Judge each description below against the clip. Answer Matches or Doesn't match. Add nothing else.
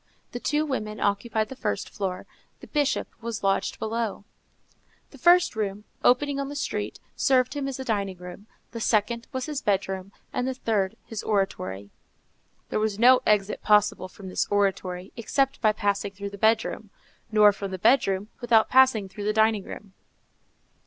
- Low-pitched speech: Doesn't match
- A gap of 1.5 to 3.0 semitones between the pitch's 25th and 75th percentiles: Doesn't match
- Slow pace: Doesn't match